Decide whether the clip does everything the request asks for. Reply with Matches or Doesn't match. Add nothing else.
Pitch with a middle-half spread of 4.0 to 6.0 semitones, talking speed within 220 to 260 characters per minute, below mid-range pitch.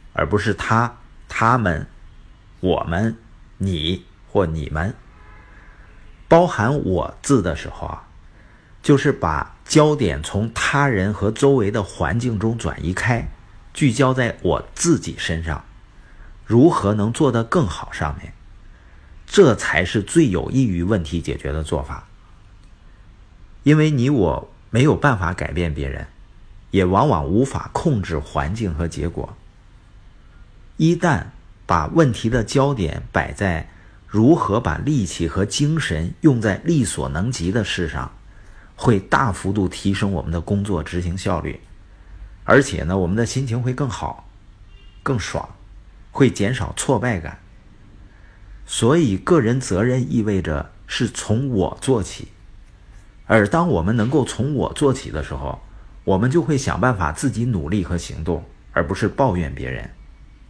Doesn't match